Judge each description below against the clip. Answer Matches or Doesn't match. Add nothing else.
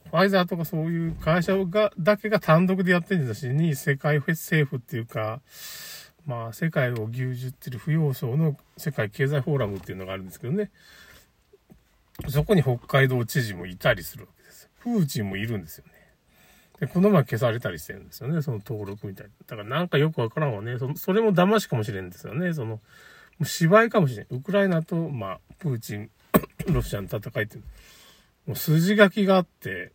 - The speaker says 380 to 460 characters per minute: Matches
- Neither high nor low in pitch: Matches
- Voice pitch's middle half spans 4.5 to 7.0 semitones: Matches